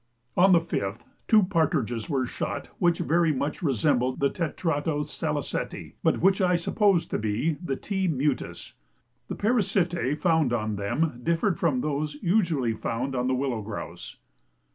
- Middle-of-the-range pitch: Yes, medium, 150 Hz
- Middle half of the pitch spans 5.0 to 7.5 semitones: Yes, average, 5.3 semitones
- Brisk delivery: No, average, 150 wpm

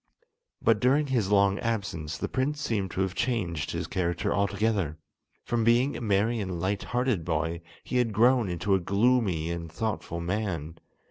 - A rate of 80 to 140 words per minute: No, average, 165 wpm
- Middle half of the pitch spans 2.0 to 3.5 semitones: No, average, 5.3 semitones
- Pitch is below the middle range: Yes, low, 100 Hz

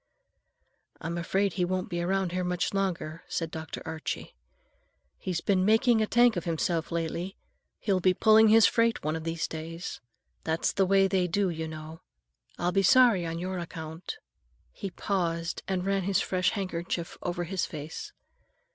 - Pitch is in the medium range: Yes, medium, 180 Hz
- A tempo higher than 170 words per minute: No, average, 165 wpm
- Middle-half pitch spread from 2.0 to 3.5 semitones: Yes, average, 2.7 semitones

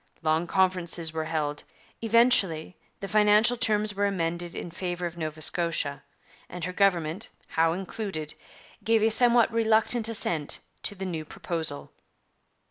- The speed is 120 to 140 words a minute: Yes, slow, 135 wpm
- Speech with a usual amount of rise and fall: Yes, average, 4.7 semitones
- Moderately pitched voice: Yes, medium, 180 Hz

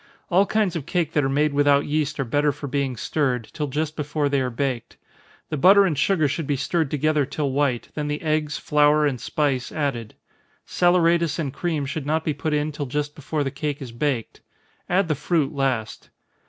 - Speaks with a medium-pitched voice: Yes, medium, 150 Hz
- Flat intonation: Yes, narrow, 2.1 semitones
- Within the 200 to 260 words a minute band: Yes, fast, 205 wpm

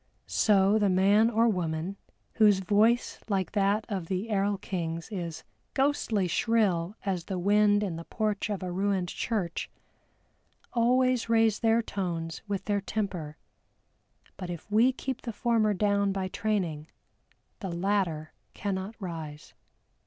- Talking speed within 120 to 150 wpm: Yes, average, 140 wpm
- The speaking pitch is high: Yes, high, 200 Hz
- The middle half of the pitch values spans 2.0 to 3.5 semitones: Yes, average, 3.2 semitones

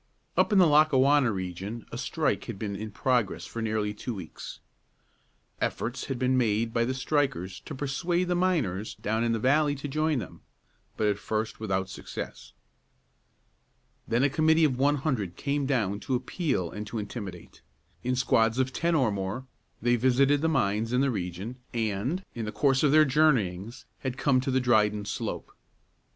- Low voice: Yes, low, 125 Hz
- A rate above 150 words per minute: Yes, average, 175 wpm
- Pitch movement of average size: Yes, average, 5.0 semitones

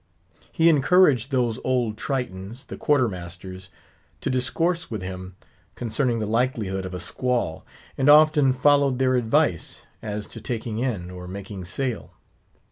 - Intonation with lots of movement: Yes, wide, 5.7 semitones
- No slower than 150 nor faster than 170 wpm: No, average, 140 wpm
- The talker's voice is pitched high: No, low, 120 Hz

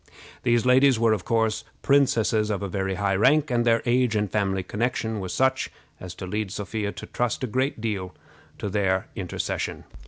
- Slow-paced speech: No, average, 180 wpm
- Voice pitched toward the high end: No, low, 110 Hz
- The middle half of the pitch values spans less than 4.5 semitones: Yes, average, 3.7 semitones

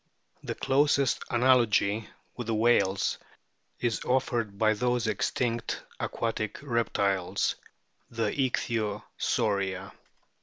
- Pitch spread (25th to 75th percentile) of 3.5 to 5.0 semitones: No, average, 2.9 semitones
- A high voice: No, low, 115 Hz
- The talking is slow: Yes, slow, 85 wpm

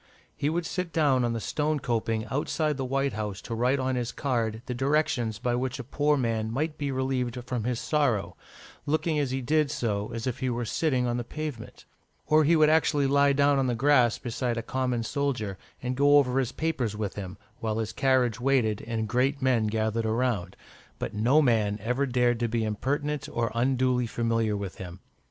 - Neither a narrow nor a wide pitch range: Yes, average, 3.6 semitones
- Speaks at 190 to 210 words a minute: Yes, average, 200 wpm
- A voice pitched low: Yes, low, 125 Hz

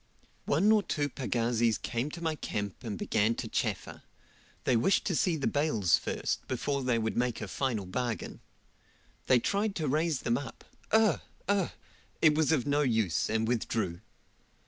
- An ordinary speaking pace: Yes, average, 170 wpm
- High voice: No, low, 125 Hz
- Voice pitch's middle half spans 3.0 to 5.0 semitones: No, wide, 5.6 semitones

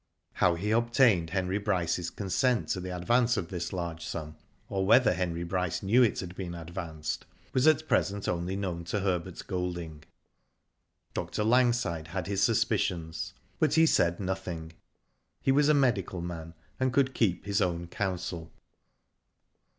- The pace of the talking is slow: No, average, 150 wpm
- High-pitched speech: No, very low, 95 Hz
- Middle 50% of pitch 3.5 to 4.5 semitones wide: Yes, average, 4.1 semitones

